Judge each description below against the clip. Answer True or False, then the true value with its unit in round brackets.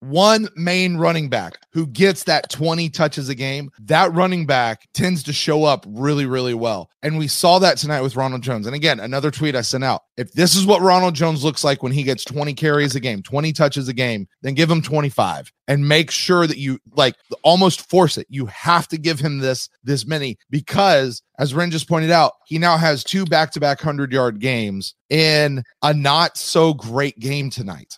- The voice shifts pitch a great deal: False (3.7 semitones)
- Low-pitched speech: False (150 Hz)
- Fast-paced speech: True (210 wpm)